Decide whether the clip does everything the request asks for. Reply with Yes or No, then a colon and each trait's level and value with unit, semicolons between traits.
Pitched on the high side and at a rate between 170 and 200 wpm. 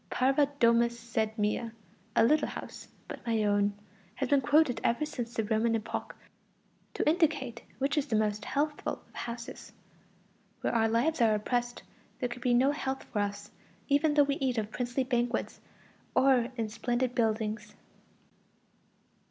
No: high, 240 Hz; average, 155 wpm